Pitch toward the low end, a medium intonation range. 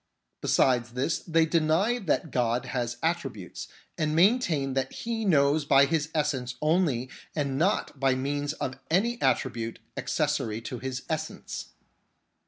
No: medium, 145 Hz; average, 4.0 semitones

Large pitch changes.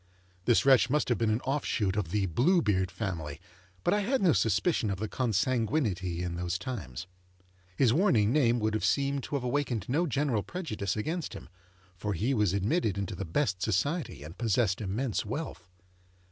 Yes: wide, 6.3 semitones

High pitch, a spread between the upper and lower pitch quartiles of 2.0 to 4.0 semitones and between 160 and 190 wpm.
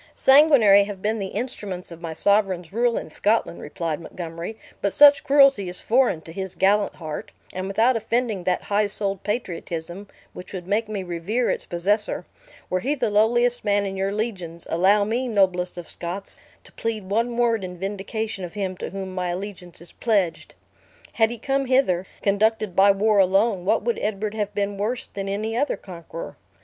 Yes: high, 200 Hz; average, 3.4 semitones; average, 180 wpm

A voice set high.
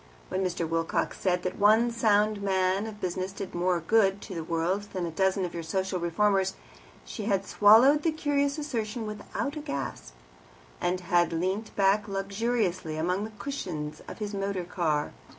Yes: high, 195 Hz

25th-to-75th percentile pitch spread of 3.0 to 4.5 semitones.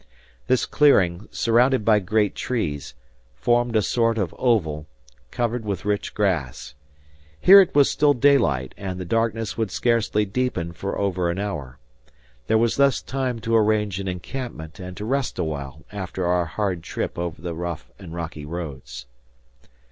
No: wide, 5.4 semitones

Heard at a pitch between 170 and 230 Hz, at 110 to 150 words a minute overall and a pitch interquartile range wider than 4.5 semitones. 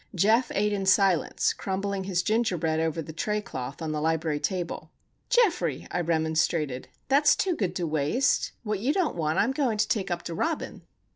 No: high, 190 Hz; average, 195 wpm; average, 5.3 semitones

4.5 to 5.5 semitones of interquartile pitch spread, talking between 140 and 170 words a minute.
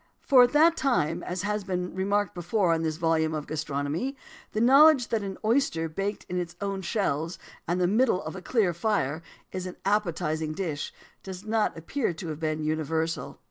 No: average, 4.9 semitones; average, 185 wpm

